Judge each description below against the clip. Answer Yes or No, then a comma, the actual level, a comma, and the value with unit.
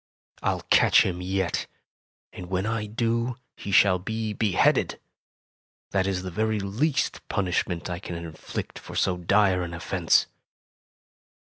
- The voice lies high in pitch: No, very low, 95 Hz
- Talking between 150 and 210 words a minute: No, slow, 135 wpm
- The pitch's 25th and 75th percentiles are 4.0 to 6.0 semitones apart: No, average, 3.0 semitones